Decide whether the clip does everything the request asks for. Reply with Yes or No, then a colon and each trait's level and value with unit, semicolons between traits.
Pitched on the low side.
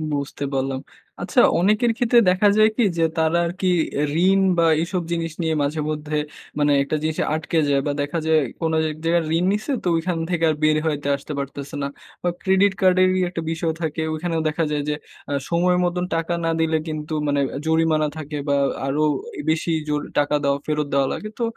No: medium, 160 Hz